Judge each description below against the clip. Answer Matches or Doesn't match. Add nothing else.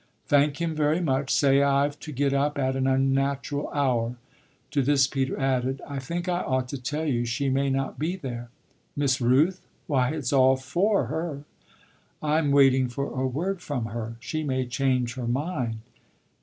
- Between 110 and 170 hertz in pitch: Matches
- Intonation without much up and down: Matches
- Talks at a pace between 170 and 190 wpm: Matches